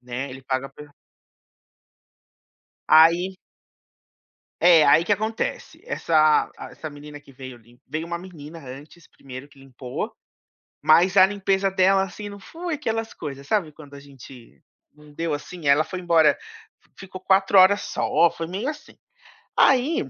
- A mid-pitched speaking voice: Yes, medium, 165 Hz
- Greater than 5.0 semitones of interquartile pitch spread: Yes, wide, 5.4 semitones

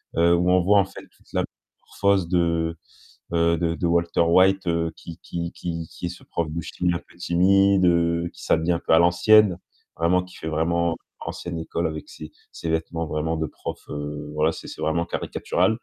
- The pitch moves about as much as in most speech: No, narrow, 1.4 semitones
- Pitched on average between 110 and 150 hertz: No, very low, 85 Hz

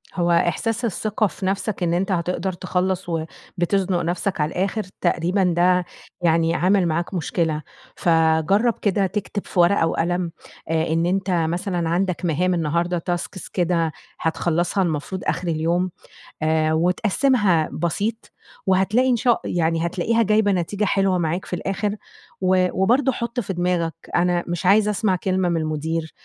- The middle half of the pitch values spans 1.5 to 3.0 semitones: Yes, average, 2.7 semitones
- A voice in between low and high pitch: Yes, medium, 180 Hz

